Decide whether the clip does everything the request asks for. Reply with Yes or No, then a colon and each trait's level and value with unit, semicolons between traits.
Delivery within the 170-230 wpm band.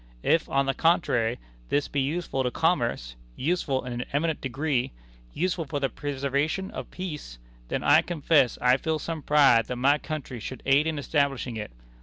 Yes: average, 175 wpm